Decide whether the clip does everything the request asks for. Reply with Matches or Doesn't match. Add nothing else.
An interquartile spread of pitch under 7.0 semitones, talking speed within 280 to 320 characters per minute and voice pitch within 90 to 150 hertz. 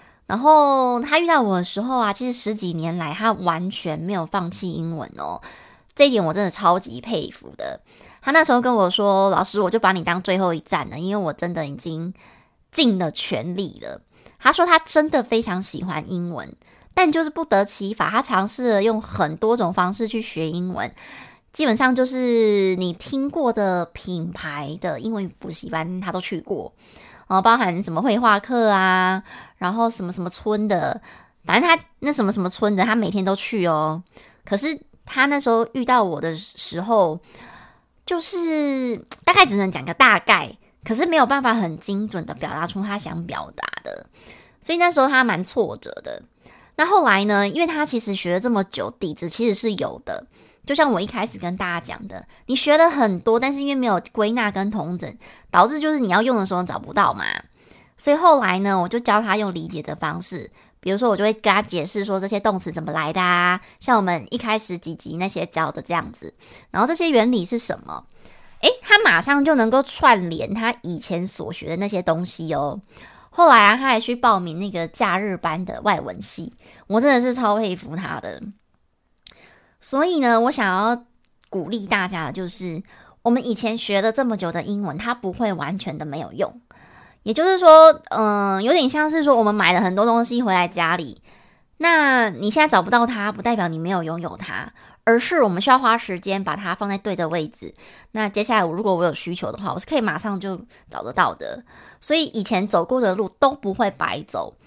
Doesn't match